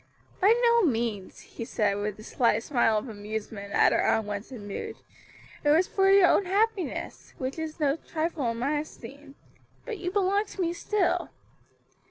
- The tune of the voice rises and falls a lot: Yes, wide, 8.9 semitones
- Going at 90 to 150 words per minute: No, average, 170 wpm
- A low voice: No, very high, 290 Hz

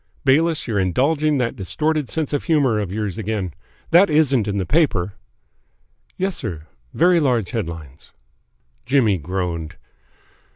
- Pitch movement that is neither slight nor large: No, wide, 8.3 semitones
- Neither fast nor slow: No, slow, 130 wpm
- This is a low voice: Yes, low, 115 Hz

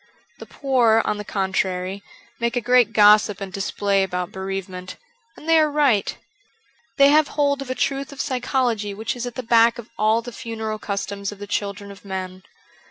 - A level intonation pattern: No, average, 4.1 semitones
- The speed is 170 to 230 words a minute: Yes, average, 185 wpm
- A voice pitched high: Yes, high, 215 Hz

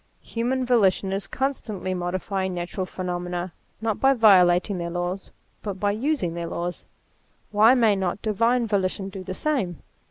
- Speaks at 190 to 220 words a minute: No, average, 155 wpm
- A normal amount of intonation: Yes, average, 4.0 semitones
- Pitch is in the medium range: No, high, 195 Hz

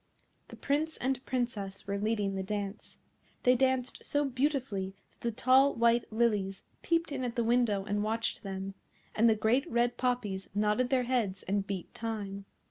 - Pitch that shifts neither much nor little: Yes, average, 4.0 semitones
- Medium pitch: No, high, 230 Hz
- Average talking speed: Yes, average, 170 wpm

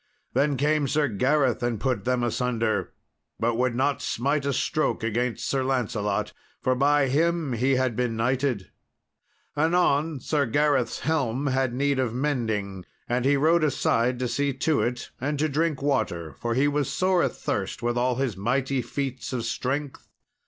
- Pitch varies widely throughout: No, average, 3.2 semitones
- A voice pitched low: Yes, low, 130 Hz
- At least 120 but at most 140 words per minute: No, average, 165 wpm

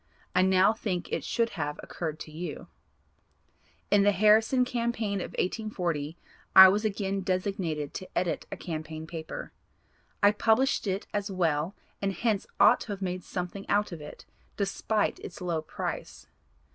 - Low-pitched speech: No, high, 190 Hz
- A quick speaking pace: No, average, 155 wpm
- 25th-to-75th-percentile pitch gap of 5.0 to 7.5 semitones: No, average, 3.5 semitones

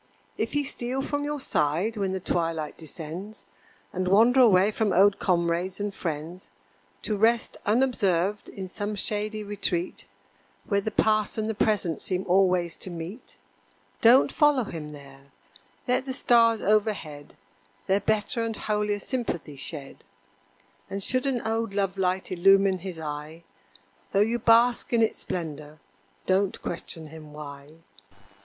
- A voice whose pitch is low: No, high, 195 Hz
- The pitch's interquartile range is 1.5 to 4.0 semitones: No, average, 4.7 semitones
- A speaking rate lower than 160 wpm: Yes, average, 145 wpm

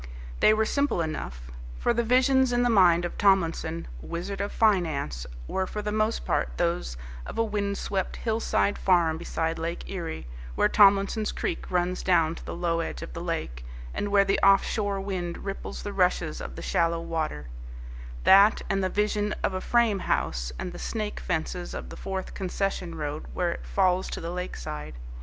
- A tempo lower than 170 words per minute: No, average, 185 wpm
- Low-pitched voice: No, medium, 185 Hz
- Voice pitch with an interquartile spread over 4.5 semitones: No, average, 3.5 semitones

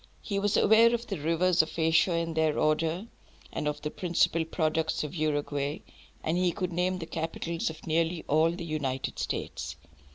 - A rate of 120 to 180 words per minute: Yes, average, 175 wpm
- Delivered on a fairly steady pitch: Yes, narrow, 2.3 semitones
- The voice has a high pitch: No, medium, 165 Hz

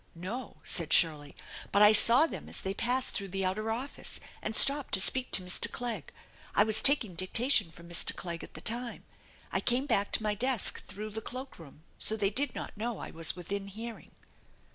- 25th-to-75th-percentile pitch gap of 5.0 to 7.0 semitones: No, average, 4.6 semitones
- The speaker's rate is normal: No, fast, 210 wpm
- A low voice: No, high, 215 Hz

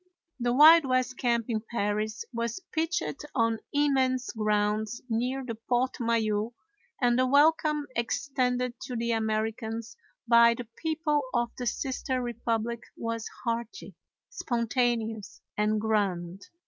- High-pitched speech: Yes, high, 235 Hz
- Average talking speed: No, slow, 120 wpm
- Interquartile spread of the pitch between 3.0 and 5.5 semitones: No, narrow, 2.5 semitones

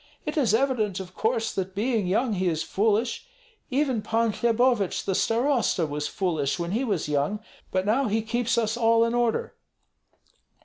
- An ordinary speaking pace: Yes, average, 170 wpm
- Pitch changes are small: No, average, 4.0 semitones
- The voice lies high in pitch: Yes, high, 225 Hz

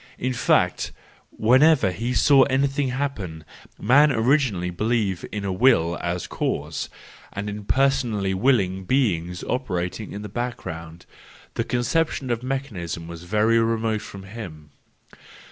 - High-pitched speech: No, low, 110 Hz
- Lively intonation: Yes, wide, 5.8 semitones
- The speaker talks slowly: Yes, slow, 130 wpm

